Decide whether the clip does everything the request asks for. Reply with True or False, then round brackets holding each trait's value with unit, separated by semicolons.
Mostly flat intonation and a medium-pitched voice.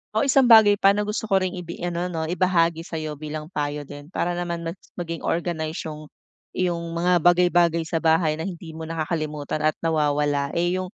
True (2.3 semitones; 170 Hz)